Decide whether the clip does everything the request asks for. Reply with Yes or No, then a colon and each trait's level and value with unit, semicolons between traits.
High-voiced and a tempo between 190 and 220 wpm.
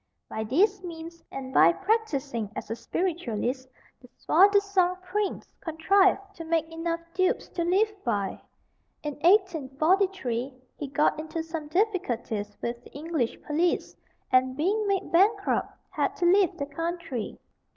No: very high, 330 Hz; average, 140 wpm